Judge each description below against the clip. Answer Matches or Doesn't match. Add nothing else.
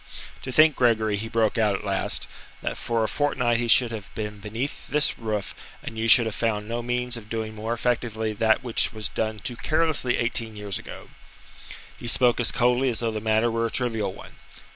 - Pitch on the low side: Matches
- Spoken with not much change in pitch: Matches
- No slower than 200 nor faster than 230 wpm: Matches